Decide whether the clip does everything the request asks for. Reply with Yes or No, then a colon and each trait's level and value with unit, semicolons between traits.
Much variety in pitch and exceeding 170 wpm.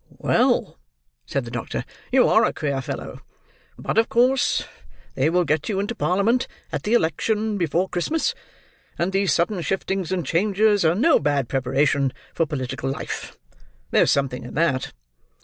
No: wide, 6.6 semitones; average, 155 wpm